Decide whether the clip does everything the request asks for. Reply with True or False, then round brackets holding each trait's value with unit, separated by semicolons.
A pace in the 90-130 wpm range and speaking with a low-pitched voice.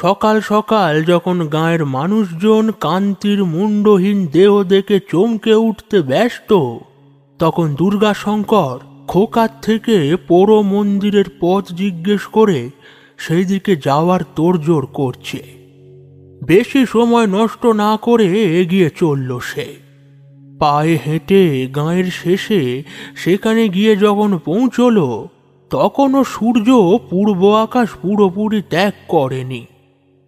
False (95 wpm; 190 Hz)